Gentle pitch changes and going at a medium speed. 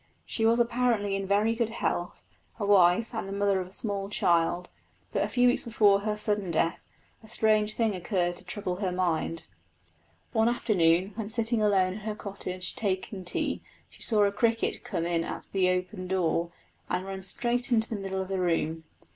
No: average, 3.3 semitones; average, 190 wpm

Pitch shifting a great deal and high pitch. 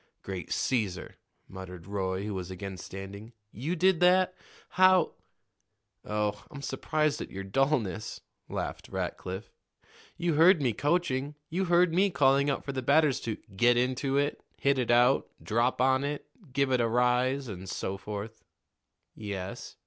No: wide, 6.3 semitones; low, 125 Hz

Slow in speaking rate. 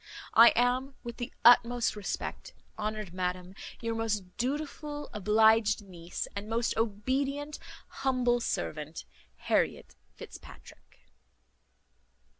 Yes: slow, 95 wpm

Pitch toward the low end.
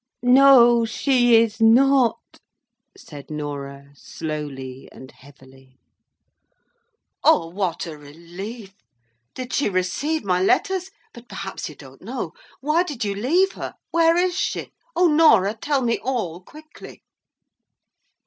No: high, 220 Hz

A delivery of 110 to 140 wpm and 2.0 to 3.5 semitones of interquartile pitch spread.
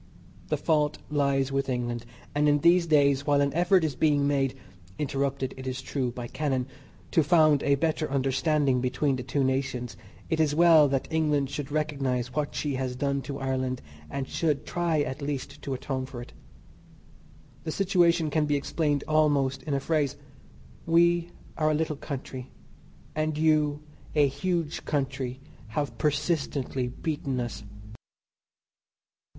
No: average, 155 wpm; narrow, 2.6 semitones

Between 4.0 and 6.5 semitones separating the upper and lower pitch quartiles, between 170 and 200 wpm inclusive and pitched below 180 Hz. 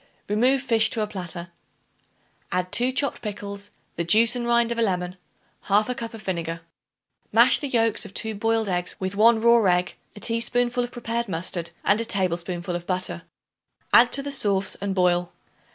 No: average, 4.4 semitones; average, 180 wpm; high, 210 Hz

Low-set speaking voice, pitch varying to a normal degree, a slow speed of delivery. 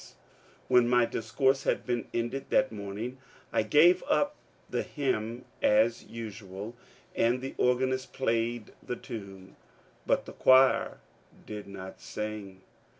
Yes: low, 115 Hz; average, 3.5 semitones; slow, 120 wpm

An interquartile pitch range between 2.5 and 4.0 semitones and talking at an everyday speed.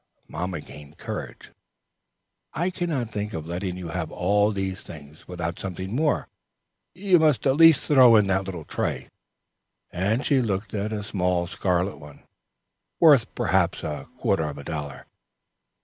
No: wide, 5.6 semitones; average, 155 wpm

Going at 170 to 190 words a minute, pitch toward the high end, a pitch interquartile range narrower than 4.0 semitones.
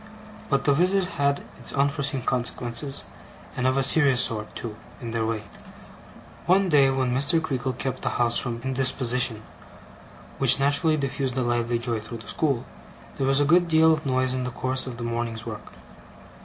No: average, 180 wpm; low, 130 Hz; average, 3.0 semitones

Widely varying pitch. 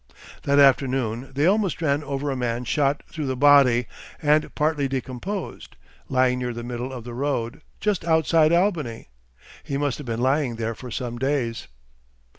No: average, 3.3 semitones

